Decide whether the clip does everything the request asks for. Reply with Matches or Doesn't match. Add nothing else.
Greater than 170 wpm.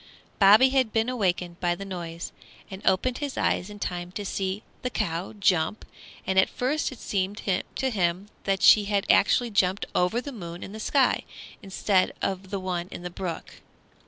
Matches